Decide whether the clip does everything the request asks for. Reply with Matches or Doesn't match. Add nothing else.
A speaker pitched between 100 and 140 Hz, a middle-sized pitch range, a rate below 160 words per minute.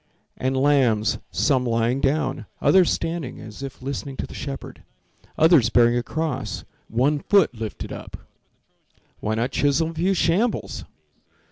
Matches